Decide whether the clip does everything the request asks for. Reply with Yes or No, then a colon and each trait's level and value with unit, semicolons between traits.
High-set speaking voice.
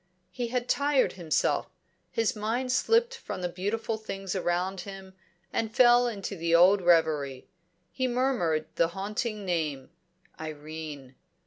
Yes: high, 195 Hz